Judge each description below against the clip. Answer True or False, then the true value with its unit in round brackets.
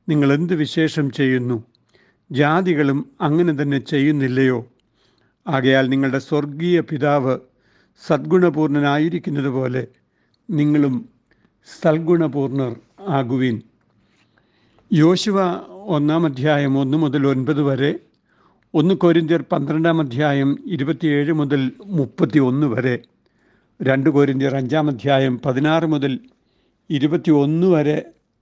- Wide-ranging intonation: False (3.0 semitones)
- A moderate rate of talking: True (85 wpm)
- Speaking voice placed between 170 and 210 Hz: False (145 Hz)